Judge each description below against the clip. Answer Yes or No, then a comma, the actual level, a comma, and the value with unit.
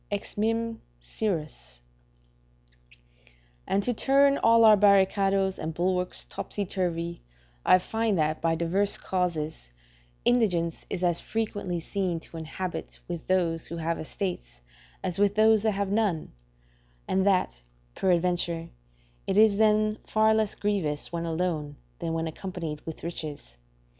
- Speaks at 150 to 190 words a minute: No, slow, 135 wpm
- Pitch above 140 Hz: Yes, medium, 185 Hz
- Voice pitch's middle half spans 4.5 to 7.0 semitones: No, average, 3.9 semitones